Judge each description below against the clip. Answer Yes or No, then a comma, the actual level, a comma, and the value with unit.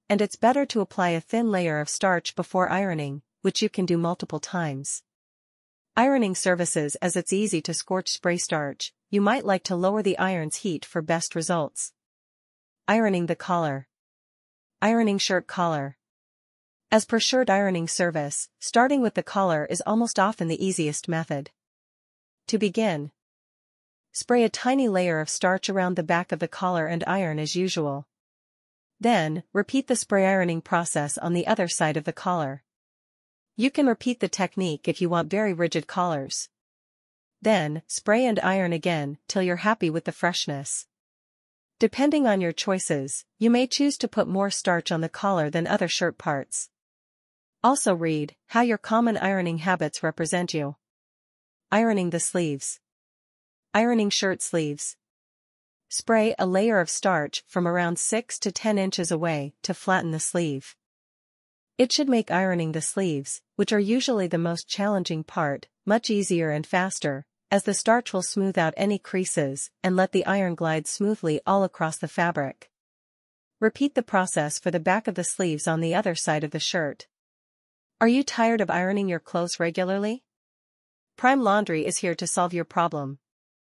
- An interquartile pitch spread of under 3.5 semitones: No, average, 3.9 semitones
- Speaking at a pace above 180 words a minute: No, average, 165 wpm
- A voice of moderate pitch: Yes, medium, 180 Hz